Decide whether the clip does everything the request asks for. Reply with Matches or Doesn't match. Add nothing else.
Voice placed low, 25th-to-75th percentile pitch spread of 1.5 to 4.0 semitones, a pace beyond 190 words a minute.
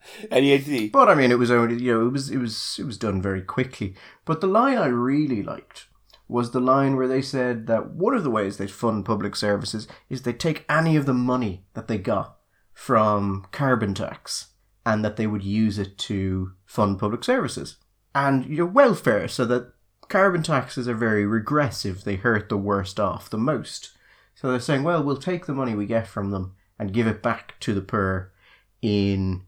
Doesn't match